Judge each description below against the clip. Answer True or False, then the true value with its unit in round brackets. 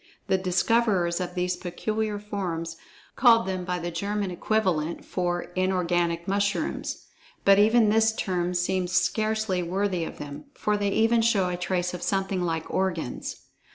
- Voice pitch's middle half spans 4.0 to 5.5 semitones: False (2.8 semitones)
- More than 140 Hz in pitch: True (185 Hz)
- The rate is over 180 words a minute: False (150 wpm)